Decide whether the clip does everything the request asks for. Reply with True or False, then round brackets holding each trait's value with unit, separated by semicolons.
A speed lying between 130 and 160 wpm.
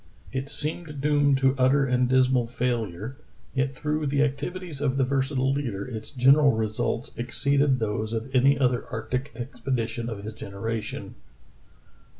True (155 wpm)